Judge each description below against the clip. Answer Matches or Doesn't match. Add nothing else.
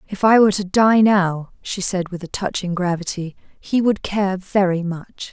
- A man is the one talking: Doesn't match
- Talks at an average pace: Matches